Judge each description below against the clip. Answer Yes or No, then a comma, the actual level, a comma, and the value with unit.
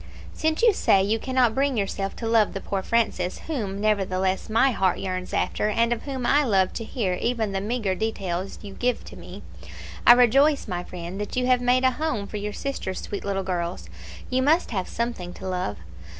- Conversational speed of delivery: No, fast, 210 wpm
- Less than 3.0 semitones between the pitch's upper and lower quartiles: No, average, 4.6 semitones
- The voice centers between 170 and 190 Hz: No, high, 215 Hz